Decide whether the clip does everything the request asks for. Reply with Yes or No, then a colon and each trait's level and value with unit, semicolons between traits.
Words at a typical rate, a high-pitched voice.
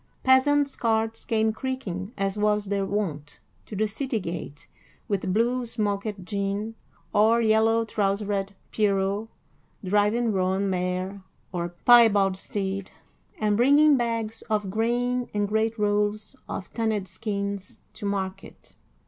No: slow, 125 wpm; high, 210 Hz